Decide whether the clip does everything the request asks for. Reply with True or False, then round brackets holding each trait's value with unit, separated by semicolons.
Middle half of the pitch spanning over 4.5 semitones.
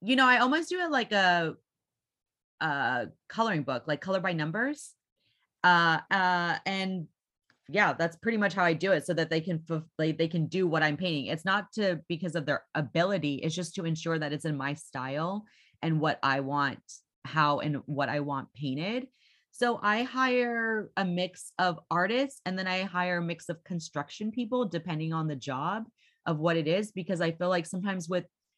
False (3.6 semitones)